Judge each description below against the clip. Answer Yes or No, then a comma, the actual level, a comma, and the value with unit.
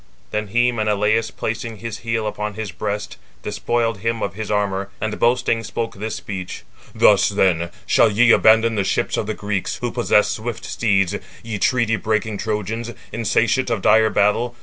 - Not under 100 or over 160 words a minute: No, average, 170 wpm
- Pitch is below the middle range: Yes, low, 110 Hz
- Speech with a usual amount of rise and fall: No, narrow, 1.9 semitones